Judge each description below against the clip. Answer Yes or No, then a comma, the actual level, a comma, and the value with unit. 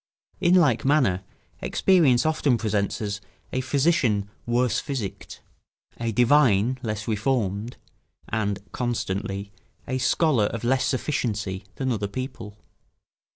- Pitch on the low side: Yes, low, 120 Hz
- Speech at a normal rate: No, slow, 110 wpm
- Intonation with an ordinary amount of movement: Yes, average, 4.3 semitones